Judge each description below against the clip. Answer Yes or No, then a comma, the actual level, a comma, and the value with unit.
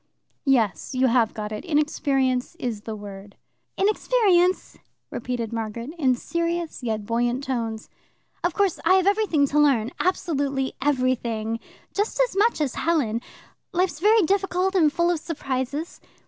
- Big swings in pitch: Yes, wide, 6.9 semitones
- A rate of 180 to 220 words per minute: No, average, 140 wpm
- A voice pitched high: Yes, very high, 280 Hz